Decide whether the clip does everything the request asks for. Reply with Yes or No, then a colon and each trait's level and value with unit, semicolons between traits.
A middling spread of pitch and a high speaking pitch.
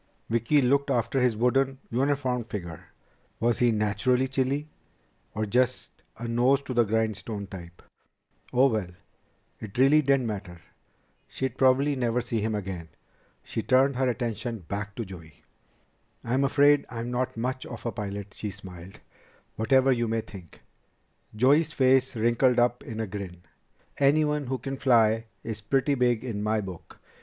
No: average, 3.7 semitones; low, 120 Hz